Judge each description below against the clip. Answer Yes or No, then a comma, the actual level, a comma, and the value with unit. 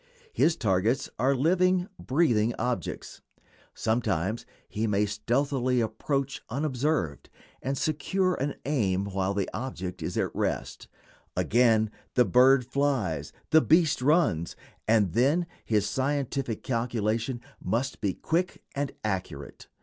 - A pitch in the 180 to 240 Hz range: No, low, 125 Hz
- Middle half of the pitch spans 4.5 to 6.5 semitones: Yes, average, 5.0 semitones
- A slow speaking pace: Yes, slow, 120 wpm